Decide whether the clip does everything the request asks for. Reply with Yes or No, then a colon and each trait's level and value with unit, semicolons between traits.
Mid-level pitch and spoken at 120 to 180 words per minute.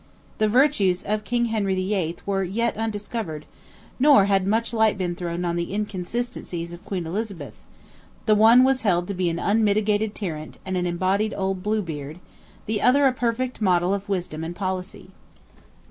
No: high, 200 Hz; average, 165 wpm